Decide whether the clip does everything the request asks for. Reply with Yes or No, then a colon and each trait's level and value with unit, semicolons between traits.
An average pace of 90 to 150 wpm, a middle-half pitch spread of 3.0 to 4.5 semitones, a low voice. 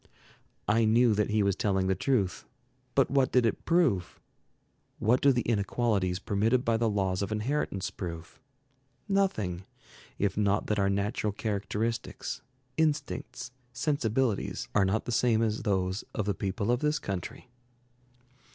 Yes: average, 145 wpm; average, 3.7 semitones; low, 110 Hz